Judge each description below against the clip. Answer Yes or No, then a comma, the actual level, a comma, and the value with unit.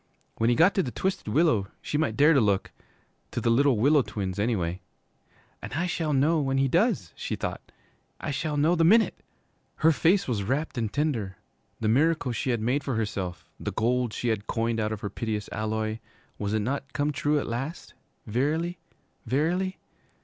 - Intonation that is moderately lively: No, wide, 6.0 semitones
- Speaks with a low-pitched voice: Yes, low, 130 Hz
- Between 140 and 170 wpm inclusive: No, average, 190 wpm